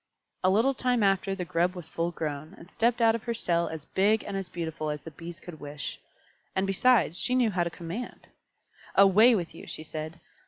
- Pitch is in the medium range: Yes, medium, 180 Hz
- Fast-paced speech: Yes, fast, 210 wpm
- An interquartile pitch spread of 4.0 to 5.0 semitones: Yes, average, 4.7 semitones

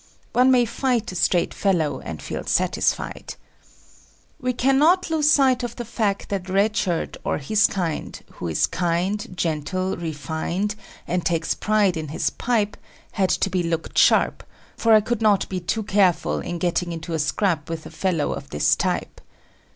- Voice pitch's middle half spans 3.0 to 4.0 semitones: No, average, 4.7 semitones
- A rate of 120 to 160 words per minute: No, average, 170 wpm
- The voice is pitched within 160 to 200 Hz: Yes, high, 190 Hz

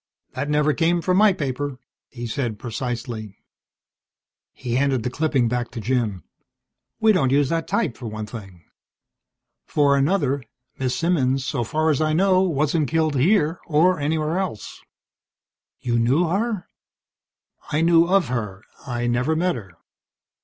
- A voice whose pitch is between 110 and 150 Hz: Yes, medium, 140 Hz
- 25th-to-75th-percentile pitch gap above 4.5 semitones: Yes, average, 5.3 semitones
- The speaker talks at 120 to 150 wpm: Yes, average, 145 wpm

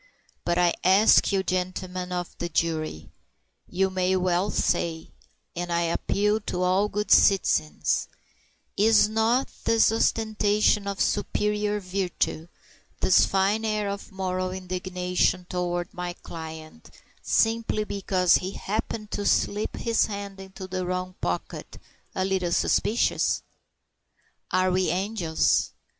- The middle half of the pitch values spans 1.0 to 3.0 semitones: Yes, narrow, 2.6 semitones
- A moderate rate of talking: No, slow, 120 wpm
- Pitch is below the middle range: No, medium, 185 Hz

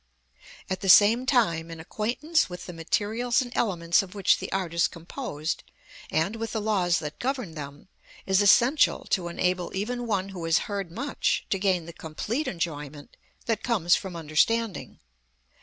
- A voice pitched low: No, high, 190 Hz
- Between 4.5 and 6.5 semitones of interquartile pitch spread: Yes, average, 5.2 semitones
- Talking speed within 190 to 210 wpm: No, average, 165 wpm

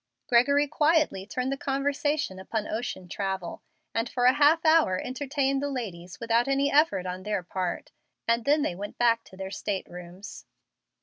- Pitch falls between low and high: No, high, 235 Hz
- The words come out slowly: No, average, 170 wpm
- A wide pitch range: Yes, wide, 6.8 semitones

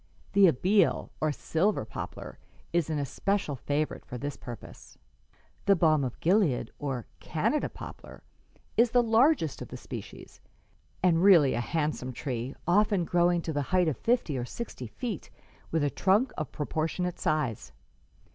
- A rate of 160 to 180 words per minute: No, average, 150 wpm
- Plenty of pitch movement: Yes, wide, 5.7 semitones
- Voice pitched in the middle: Yes, medium, 160 Hz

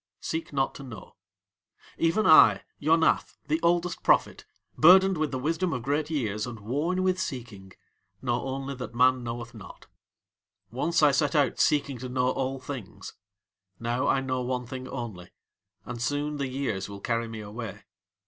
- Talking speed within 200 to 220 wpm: No, average, 165 wpm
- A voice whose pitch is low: Yes, low, 130 Hz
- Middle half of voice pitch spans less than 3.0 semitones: No, average, 4.2 semitones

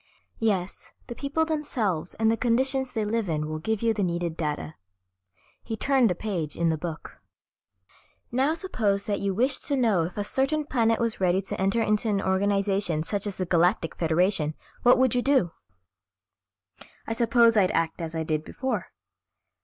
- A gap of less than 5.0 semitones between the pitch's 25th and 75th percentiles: No, wide, 5.5 semitones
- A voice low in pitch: No, high, 205 Hz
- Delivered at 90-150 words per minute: No, average, 175 wpm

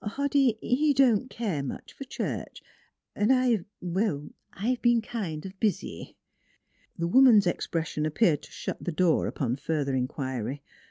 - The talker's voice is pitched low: No, high, 190 Hz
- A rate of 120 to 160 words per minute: Yes, average, 150 wpm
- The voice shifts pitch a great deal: Yes, wide, 7.9 semitones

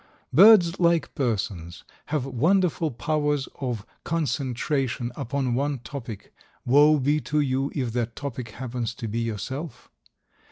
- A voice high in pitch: No, low, 135 Hz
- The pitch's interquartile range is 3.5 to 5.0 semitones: Yes, average, 4.0 semitones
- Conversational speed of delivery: No, slow, 125 wpm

